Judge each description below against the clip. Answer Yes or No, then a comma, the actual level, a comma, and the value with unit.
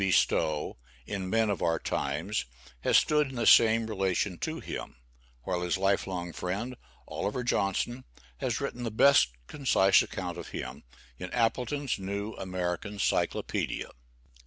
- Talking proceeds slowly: No, average, 145 wpm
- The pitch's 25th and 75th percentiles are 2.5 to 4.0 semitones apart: No, average, 4.6 semitones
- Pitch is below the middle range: Yes, low, 100 Hz